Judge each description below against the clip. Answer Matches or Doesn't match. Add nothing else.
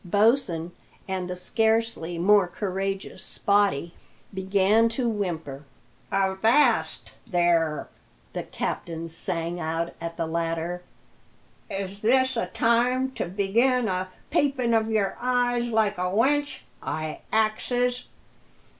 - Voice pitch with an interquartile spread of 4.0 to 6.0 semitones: Matches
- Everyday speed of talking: Doesn't match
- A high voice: Matches